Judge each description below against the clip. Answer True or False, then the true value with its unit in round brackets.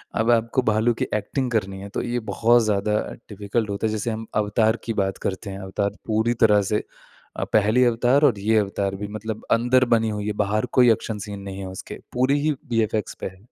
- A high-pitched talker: False (110 Hz)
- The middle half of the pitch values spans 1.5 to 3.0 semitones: True (2.5 semitones)